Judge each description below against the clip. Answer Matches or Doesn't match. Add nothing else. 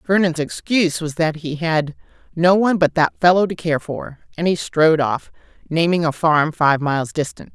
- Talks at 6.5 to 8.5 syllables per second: Doesn't match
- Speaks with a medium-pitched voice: Matches